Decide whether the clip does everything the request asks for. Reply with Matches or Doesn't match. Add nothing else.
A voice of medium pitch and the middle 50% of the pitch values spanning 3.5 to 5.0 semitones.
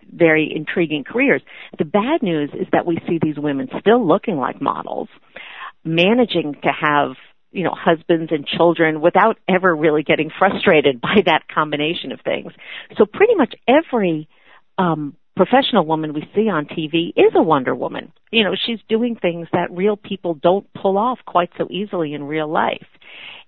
Matches